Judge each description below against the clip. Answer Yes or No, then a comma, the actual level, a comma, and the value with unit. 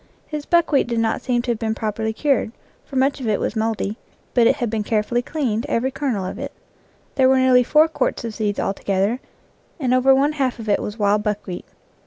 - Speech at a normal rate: No, fast, 215 wpm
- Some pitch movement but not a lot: Yes, average, 3.7 semitones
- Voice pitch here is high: Yes, high, 235 Hz